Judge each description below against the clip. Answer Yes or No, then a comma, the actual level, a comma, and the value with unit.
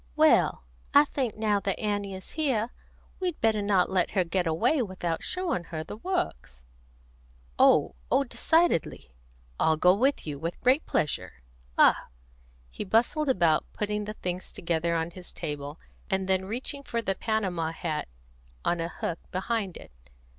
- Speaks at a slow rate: No, average, 155 wpm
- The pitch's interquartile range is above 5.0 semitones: Yes, wide, 5.6 semitones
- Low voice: No, high, 195 Hz